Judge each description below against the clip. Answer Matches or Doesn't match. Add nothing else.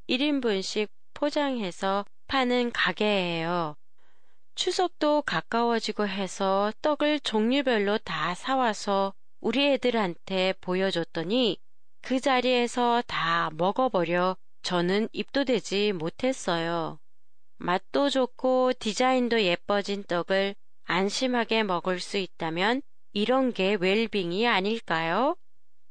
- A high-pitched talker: Matches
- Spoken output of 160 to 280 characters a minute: Matches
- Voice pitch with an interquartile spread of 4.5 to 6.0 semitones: Matches